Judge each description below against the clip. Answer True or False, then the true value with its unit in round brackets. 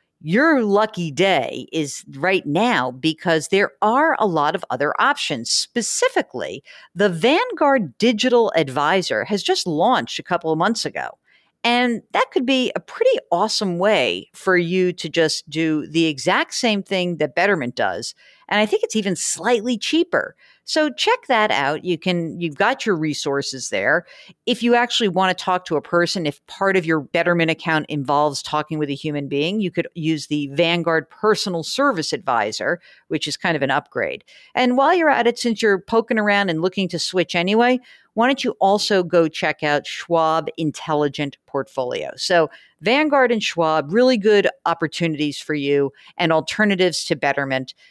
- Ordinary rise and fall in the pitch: False (6.2 semitones)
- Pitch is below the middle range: False (180 Hz)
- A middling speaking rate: True (170 wpm)